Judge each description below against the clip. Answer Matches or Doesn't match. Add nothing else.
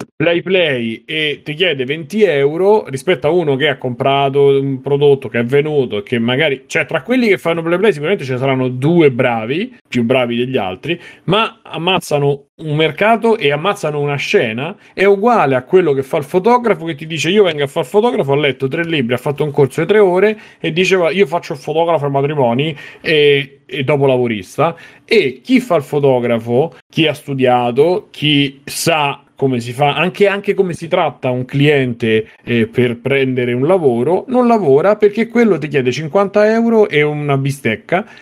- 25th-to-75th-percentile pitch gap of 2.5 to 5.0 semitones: Doesn't match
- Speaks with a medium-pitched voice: Matches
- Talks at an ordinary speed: Doesn't match